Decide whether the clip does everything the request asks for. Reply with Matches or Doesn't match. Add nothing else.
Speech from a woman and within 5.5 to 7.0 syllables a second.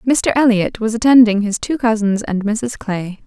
Doesn't match